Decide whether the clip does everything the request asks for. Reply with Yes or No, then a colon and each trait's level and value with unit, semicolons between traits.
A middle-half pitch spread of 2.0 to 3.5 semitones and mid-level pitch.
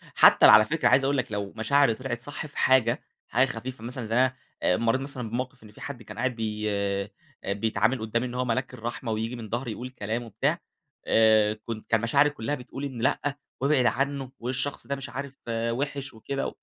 No: average, 3.2 semitones; low, 120 Hz